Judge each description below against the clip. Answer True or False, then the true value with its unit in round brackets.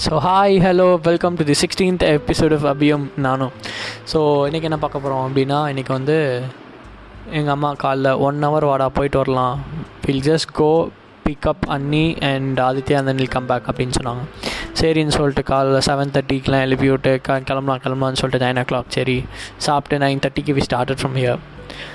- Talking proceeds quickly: True (160 wpm)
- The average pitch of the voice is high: False (135 Hz)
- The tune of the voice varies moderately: False (2.2 semitones)